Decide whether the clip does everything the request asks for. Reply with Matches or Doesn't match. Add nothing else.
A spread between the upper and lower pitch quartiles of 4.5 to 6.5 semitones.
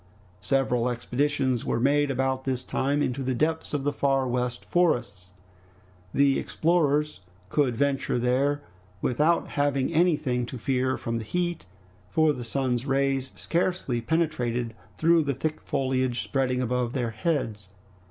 Doesn't match